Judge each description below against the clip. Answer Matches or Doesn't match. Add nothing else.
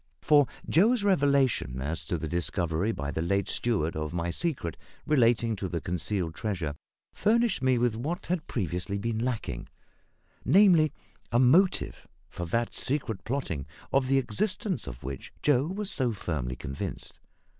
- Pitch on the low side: Matches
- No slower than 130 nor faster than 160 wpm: Matches